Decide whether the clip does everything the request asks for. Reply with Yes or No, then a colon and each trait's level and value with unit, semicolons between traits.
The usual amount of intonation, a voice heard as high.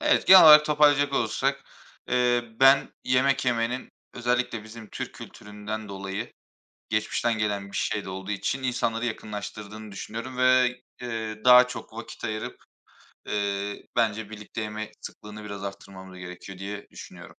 No: average, 3.2 semitones; low, 110 Hz